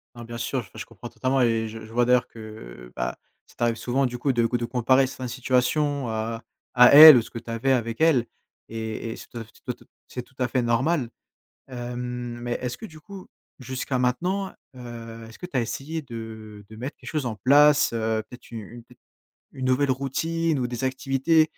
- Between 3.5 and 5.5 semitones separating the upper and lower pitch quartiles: No, average, 2.8 semitones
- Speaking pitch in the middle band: No, low, 125 Hz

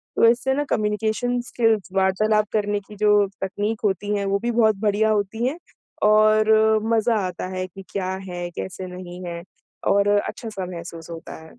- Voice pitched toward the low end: No, high, 205 Hz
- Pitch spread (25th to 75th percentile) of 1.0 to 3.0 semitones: Yes, narrow, 2.6 semitones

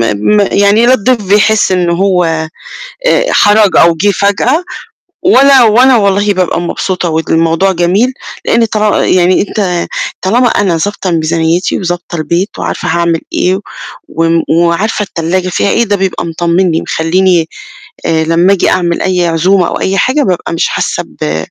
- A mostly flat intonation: No, average, 3.4 semitones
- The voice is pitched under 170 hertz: No, medium, 185 Hz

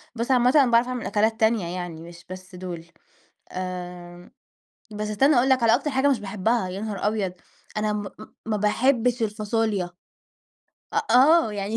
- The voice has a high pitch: Yes, high, 215 Hz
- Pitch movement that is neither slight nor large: Yes, average, 4.5 semitones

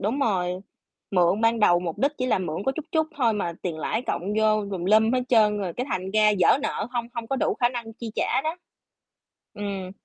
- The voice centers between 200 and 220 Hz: Yes, high, 215 Hz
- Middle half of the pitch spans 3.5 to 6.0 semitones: Yes, average, 4.2 semitones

